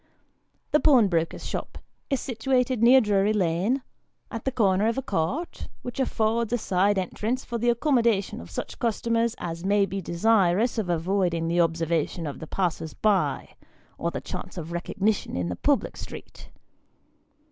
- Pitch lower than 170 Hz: No, high, 205 Hz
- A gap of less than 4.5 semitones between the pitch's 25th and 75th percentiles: No, average, 5.3 semitones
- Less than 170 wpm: Yes, average, 160 wpm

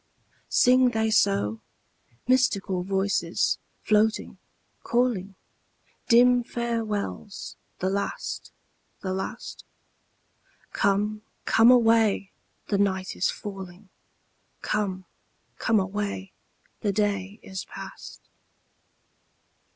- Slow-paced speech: Yes, slow, 80 wpm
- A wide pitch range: No, average, 2.8 semitones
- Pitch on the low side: No, high, 205 Hz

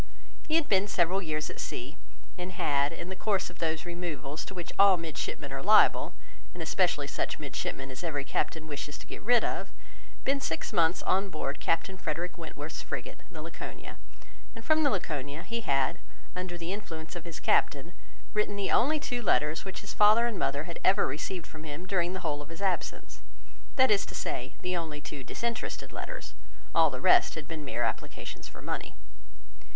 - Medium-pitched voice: Yes, medium, 175 Hz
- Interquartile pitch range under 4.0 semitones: No, average, 4.6 semitones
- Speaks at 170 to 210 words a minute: Yes, average, 190 wpm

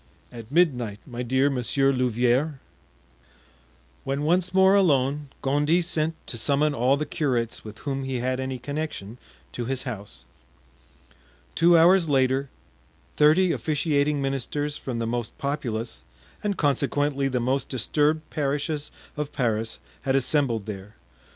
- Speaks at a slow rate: Yes, slow, 130 wpm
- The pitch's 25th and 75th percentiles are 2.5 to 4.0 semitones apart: Yes, average, 3.4 semitones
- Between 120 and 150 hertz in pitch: Yes, low, 135 Hz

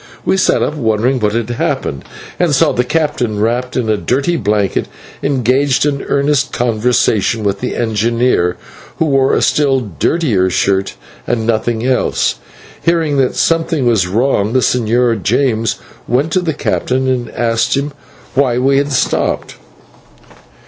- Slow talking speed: No, average, 150 wpm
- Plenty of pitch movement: No, average, 3.9 semitones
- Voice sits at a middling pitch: No, low, 125 Hz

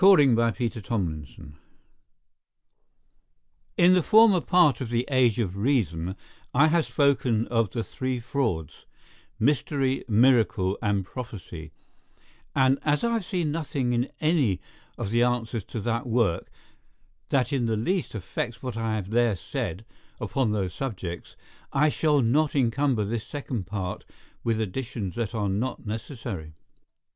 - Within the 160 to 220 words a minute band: No, average, 140 wpm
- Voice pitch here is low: Yes, low, 120 Hz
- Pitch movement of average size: Yes, average, 4.8 semitones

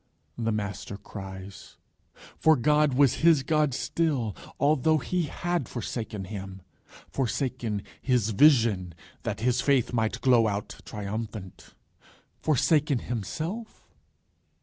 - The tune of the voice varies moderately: No, wide, 6.2 semitones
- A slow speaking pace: Yes, slow, 105 wpm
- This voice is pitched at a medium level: No, low, 120 Hz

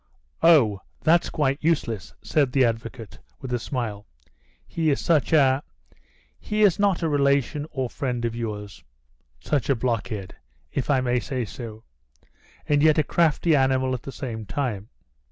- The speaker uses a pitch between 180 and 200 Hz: No, low, 130 Hz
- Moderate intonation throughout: Yes, average, 4.3 semitones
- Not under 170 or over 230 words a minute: No, average, 155 wpm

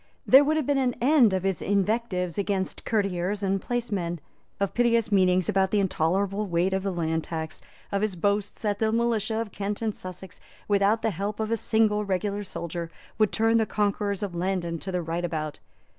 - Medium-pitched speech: No, high, 200 Hz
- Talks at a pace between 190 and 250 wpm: Yes, average, 195 wpm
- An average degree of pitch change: Yes, average, 3.1 semitones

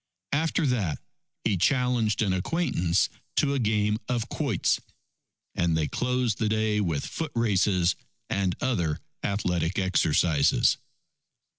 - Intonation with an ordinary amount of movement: No, wide, 5.9 semitones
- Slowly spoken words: Yes, slow, 120 wpm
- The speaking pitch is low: Yes, low, 105 Hz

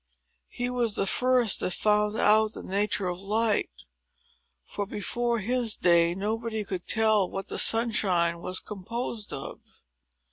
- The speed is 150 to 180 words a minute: No, average, 140 wpm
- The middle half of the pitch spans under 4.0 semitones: Yes, average, 3.2 semitones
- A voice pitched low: No, high, 210 Hz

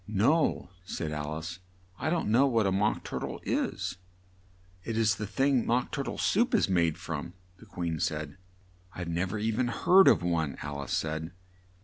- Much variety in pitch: Yes, wide, 6.2 semitones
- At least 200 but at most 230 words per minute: No, average, 190 wpm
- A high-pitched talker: No, very low, 95 Hz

